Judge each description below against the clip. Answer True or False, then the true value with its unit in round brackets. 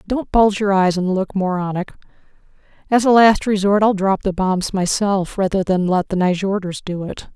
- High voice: True (195 Hz)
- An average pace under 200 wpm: True (190 wpm)